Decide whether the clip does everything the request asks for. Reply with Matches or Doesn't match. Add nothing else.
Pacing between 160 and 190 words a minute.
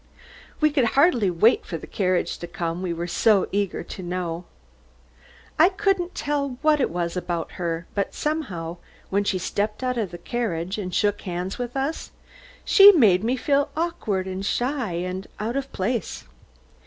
Matches